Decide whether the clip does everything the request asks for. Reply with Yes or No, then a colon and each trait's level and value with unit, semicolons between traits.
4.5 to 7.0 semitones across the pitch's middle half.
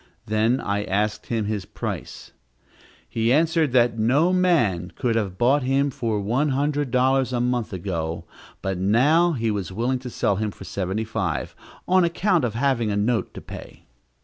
Yes: average, 4.8 semitones